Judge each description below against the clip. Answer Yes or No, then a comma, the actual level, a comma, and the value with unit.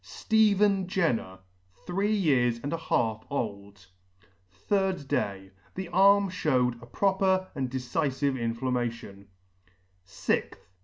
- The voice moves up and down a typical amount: No, wide, 8.3 semitones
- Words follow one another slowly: Yes, slow, 105 wpm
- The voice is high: No, medium, 140 Hz